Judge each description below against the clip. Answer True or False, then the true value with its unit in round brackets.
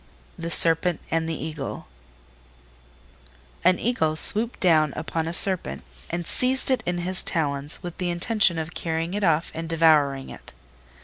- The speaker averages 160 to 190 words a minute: False (150 wpm)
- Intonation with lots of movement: False (2.4 semitones)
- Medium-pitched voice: True (165 Hz)